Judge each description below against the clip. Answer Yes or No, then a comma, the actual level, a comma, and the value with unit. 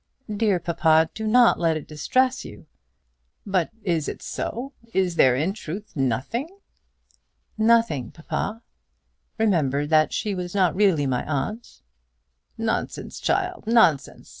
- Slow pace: Yes, slow, 125 wpm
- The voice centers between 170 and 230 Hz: Yes, medium, 185 Hz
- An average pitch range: No, wide, 6.3 semitones